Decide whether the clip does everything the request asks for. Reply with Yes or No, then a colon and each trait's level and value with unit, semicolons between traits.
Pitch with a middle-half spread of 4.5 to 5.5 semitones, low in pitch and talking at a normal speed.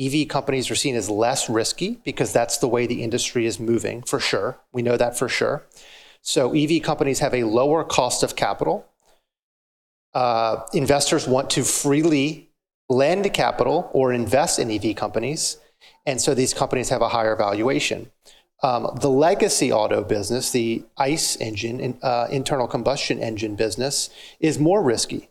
No: average, 3.7 semitones; low, 125 Hz; average, 160 wpm